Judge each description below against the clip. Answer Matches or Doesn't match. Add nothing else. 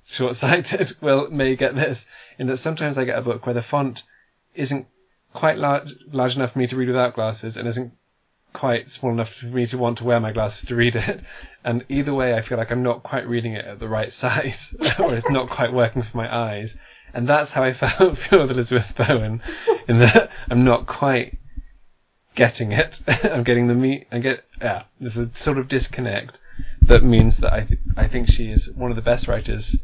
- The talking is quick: Matches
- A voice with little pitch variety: Matches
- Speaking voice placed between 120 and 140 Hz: Matches